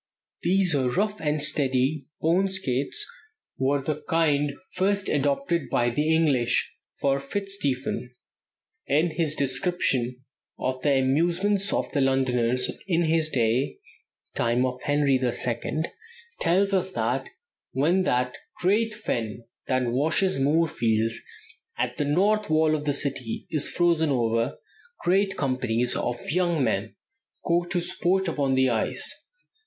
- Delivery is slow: Yes, slow, 130 wpm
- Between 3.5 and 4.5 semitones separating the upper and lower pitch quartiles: No, average, 5.3 semitones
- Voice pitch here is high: No, medium, 145 Hz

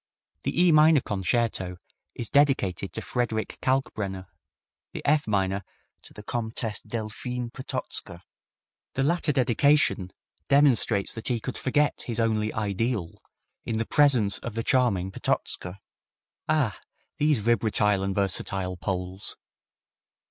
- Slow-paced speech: Yes, slow, 120 wpm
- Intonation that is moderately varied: Yes, average, 4.8 semitones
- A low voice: Yes, low, 110 Hz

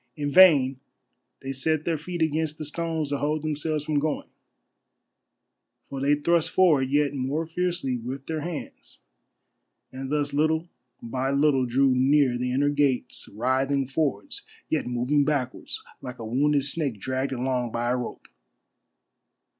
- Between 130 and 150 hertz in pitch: Yes, medium, 140 Hz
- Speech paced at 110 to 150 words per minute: Yes, average, 145 wpm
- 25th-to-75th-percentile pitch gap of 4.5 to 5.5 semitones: No, average, 3.0 semitones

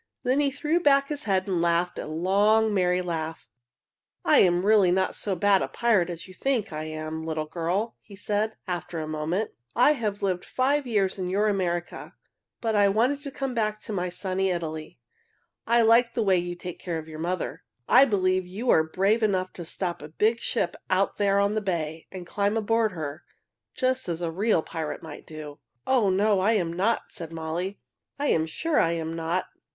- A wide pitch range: No, average, 4.5 semitones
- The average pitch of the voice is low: No, high, 190 Hz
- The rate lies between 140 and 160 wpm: No, average, 200 wpm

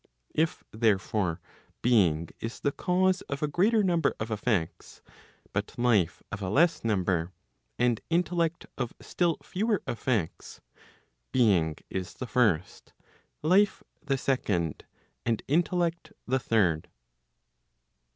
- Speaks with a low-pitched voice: Yes, low, 120 Hz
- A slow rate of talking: Yes, slow, 115 wpm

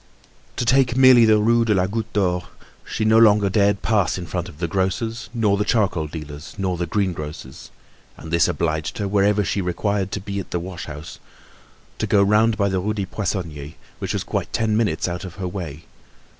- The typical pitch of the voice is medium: No, low, 100 Hz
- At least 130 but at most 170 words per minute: No, fast, 205 wpm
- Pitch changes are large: No, average, 3.6 semitones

